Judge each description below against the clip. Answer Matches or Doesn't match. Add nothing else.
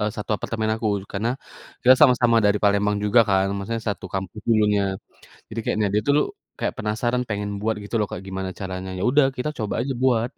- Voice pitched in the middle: Doesn't match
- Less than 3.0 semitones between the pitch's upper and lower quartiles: Matches